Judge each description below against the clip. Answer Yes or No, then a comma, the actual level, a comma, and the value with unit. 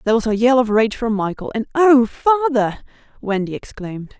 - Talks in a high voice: Yes, high, 235 Hz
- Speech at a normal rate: Yes, average, 185 wpm